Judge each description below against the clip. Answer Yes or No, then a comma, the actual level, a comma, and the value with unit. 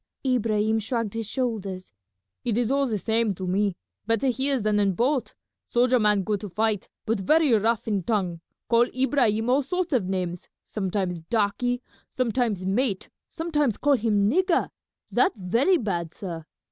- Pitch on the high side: Yes, high, 225 Hz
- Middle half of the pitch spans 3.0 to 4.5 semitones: Yes, average, 4.2 semitones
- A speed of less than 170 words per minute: Yes, average, 160 wpm